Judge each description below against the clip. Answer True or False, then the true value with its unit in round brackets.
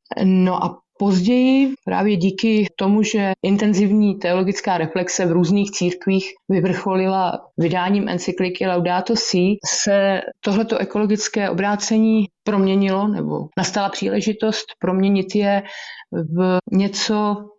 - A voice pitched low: False (195 Hz)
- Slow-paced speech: True (100 wpm)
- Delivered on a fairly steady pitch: True (2.1 semitones)